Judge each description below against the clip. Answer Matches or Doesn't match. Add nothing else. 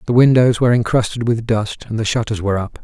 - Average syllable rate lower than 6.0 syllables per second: Doesn't match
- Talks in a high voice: Doesn't match